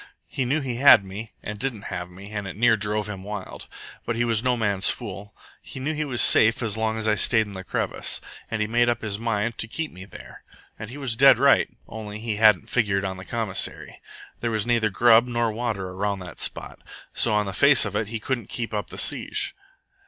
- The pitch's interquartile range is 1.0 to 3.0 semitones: Yes, narrow, 2.6 semitones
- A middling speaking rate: No, fast, 230 wpm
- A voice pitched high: No, low, 110 Hz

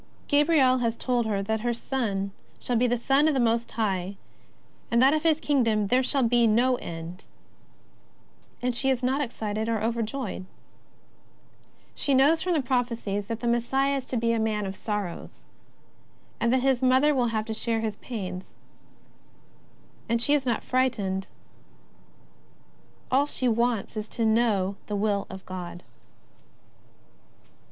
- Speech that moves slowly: No, average, 160 wpm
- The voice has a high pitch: Yes, high, 235 Hz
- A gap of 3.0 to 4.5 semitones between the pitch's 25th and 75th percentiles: Yes, average, 3.5 semitones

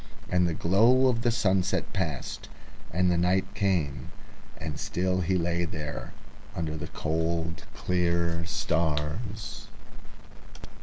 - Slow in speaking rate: Yes, slow, 115 wpm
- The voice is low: Yes, very low, 85 Hz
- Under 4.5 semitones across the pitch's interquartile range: Yes, narrow, 2.5 semitones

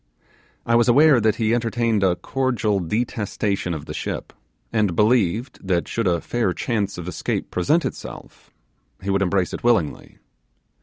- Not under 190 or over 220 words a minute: No, average, 155 wpm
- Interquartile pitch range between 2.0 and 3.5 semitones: No, average, 4.1 semitones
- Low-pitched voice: Yes, low, 110 Hz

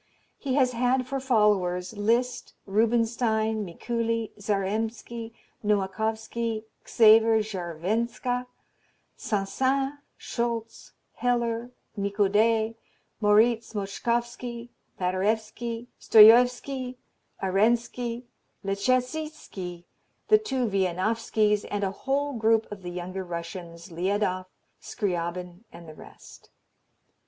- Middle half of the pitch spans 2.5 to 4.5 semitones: Yes, average, 3.4 semitones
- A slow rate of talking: Yes, slow, 85 wpm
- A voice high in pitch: Yes, high, 220 Hz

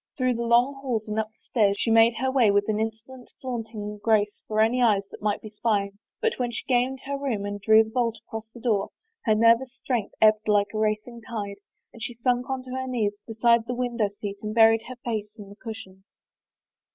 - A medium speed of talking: No, fast, 225 wpm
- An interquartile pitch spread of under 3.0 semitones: Yes, narrow, 2.5 semitones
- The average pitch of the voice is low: No, high, 225 Hz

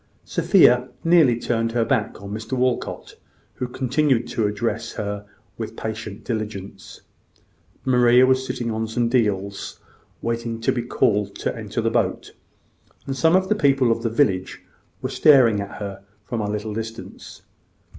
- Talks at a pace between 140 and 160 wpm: Yes, average, 155 wpm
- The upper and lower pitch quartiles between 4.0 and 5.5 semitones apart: No, average, 3.2 semitones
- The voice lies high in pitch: No, low, 115 Hz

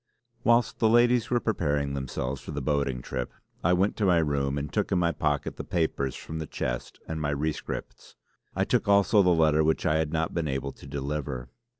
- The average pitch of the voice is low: Yes, very low, 75 Hz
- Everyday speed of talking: No, fast, 210 wpm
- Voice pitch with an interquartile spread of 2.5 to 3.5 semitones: No, average, 4.2 semitones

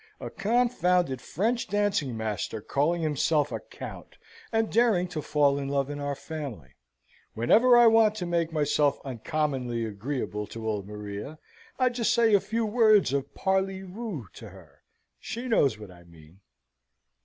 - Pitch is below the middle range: No, medium, 155 Hz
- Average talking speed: Yes, average, 155 wpm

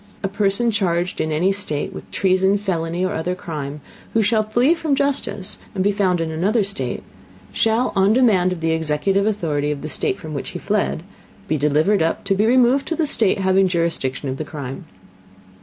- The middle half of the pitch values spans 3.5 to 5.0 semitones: Yes, average, 4.6 semitones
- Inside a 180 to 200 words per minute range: Yes, average, 195 wpm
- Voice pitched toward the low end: No, high, 190 Hz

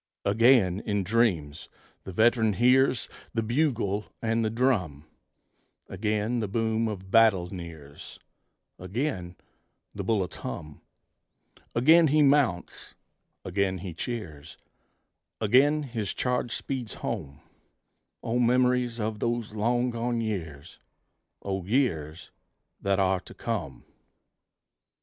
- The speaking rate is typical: No, slow, 110 wpm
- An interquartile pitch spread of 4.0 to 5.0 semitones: Yes, average, 4.6 semitones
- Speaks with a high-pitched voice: No, low, 110 Hz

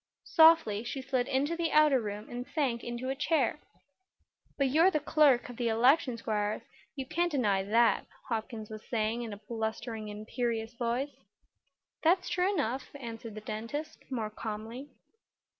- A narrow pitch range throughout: No, average, 4.4 semitones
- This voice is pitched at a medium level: No, high, 240 Hz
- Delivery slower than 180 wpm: Yes, average, 155 wpm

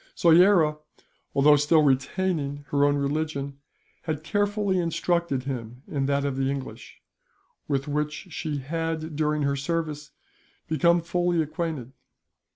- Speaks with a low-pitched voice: No, medium, 150 Hz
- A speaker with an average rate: No, slow, 125 wpm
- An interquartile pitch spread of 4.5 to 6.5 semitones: No, average, 3.1 semitones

